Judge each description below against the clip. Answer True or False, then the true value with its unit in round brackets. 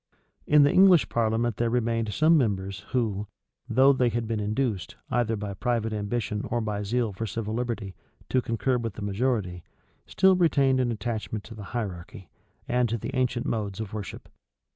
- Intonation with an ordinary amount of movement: True (3.0 semitones)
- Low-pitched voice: True (115 Hz)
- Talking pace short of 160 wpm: False (175 wpm)